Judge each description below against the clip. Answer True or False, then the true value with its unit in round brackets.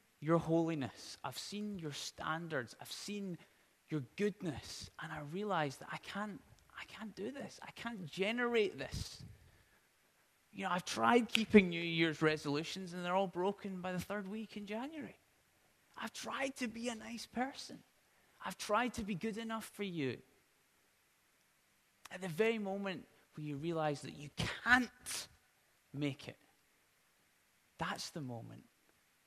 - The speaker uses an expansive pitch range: True (5.8 semitones)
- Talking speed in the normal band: True (150 wpm)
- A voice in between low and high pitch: False (195 Hz)